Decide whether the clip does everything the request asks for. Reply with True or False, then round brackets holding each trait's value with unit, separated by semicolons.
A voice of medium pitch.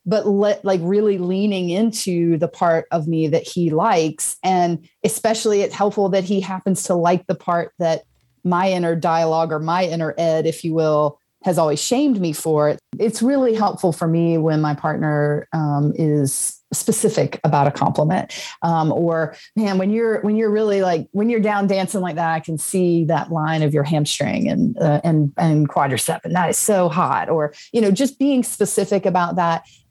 True (175 Hz)